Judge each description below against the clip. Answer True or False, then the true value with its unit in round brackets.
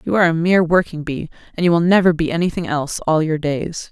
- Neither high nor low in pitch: True (165 Hz)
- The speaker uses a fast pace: True (245 wpm)